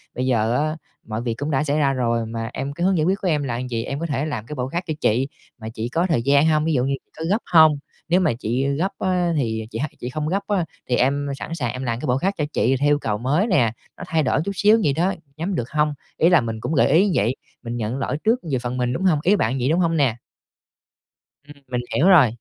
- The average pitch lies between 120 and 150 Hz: Yes, medium, 140 Hz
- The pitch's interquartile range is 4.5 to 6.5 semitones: Yes, average, 5.1 semitones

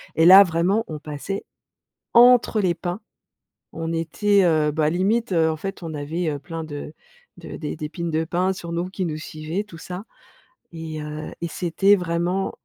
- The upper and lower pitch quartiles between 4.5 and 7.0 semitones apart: No, average, 3.2 semitones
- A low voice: No, medium, 170 Hz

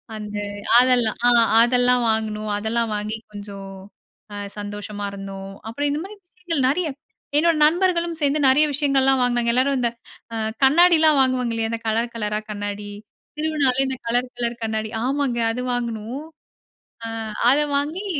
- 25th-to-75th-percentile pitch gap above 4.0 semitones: Yes, average, 4.7 semitones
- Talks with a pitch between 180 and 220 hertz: No, high, 245 Hz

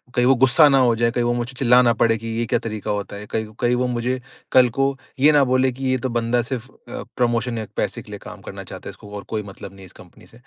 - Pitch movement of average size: No, narrow, 2.0 semitones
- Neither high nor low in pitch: No, low, 120 Hz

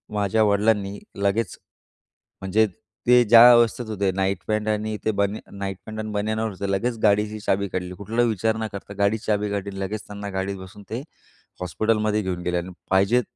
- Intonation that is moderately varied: No, narrow, 1.9 semitones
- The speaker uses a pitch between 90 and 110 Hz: Yes, low, 105 Hz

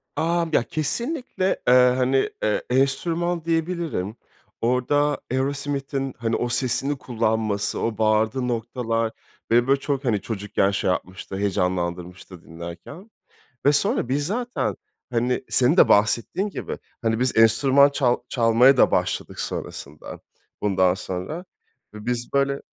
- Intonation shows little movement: No, average, 4.8 semitones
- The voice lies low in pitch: Yes, low, 125 Hz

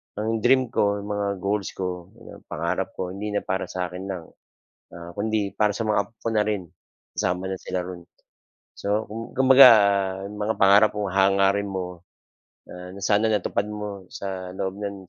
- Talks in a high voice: No, low, 100 Hz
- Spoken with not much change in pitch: Yes, narrow, 2.2 semitones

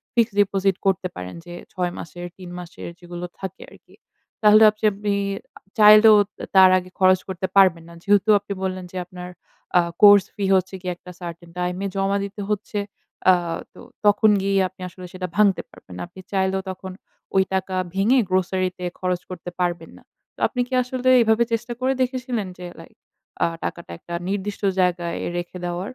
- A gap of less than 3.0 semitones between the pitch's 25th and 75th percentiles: Yes, narrow, 2.5 semitones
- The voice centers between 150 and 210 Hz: Yes, high, 190 Hz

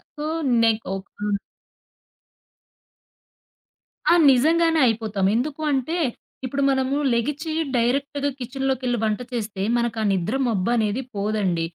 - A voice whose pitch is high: Yes, high, 240 Hz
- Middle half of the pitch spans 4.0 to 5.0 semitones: Yes, average, 4.5 semitones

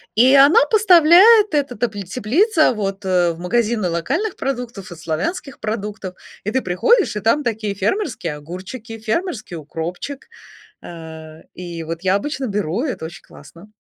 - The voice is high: Yes, high, 215 Hz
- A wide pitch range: Yes, wide, 7.6 semitones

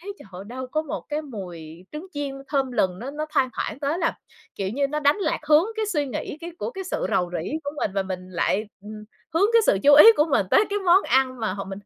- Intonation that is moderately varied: No, wide, 7.5 semitones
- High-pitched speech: Yes, very high, 275 Hz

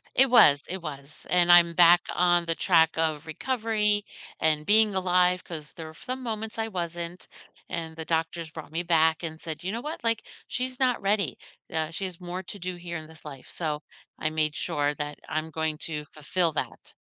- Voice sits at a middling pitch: Yes, medium, 170 Hz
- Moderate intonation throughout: Yes, average, 3.1 semitones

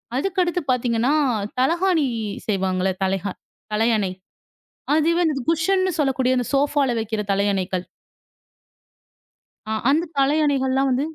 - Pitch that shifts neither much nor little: No, wide, 6.3 semitones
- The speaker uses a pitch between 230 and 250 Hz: No, very high, 265 Hz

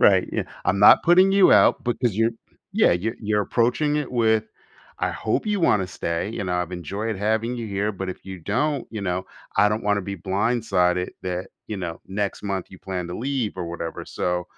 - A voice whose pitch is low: Yes, low, 100 Hz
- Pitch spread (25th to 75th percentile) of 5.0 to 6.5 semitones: No, average, 3.9 semitones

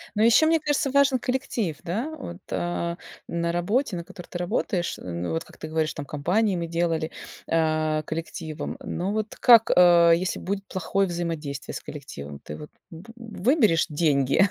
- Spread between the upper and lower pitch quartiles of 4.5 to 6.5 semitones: Yes, average, 5.3 semitones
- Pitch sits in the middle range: Yes, medium, 175 Hz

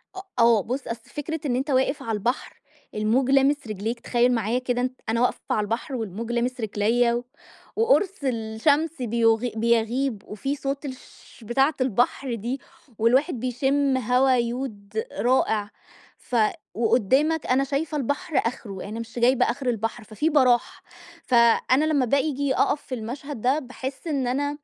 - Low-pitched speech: No, very high, 250 Hz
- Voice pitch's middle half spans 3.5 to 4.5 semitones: No, average, 3.1 semitones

